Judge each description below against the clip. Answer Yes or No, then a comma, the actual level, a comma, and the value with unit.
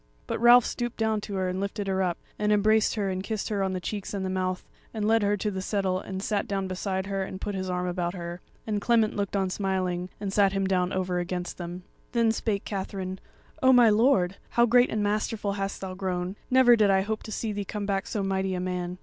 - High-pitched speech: Yes, high, 195 Hz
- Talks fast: Yes, fast, 245 wpm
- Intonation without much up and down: Yes, narrow, 2.2 semitones